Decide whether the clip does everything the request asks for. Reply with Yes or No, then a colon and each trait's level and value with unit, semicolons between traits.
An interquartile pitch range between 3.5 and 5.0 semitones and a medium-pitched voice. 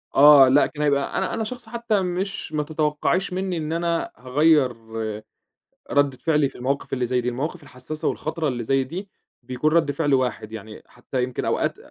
Yes: average, 4.4 semitones; medium, 145 Hz